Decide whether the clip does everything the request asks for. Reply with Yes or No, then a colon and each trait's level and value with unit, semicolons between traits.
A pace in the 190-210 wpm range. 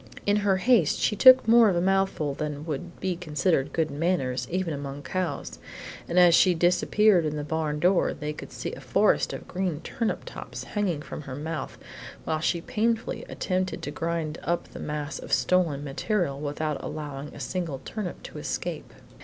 No: average, 180 wpm